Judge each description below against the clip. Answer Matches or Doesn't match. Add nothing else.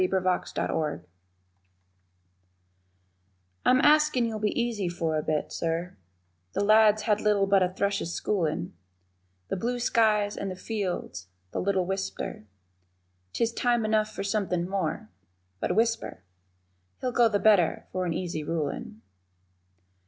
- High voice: Matches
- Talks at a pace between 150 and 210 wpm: Doesn't match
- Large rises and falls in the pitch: Doesn't match